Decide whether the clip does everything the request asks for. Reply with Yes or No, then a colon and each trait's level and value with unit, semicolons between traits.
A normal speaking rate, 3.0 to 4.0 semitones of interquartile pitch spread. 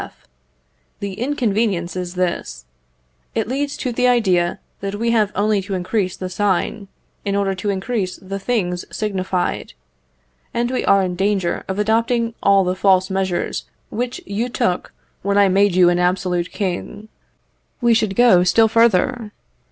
Yes: average, 155 wpm; average, 3.5 semitones